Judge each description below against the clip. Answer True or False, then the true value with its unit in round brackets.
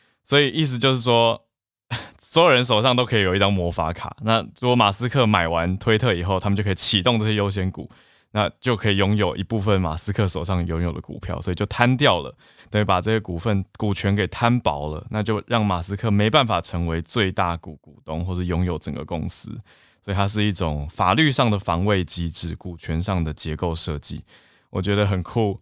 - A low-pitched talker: True (100 Hz)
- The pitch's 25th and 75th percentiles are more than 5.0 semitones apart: False (4.1 semitones)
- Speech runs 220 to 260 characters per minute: False (310 characters per minute)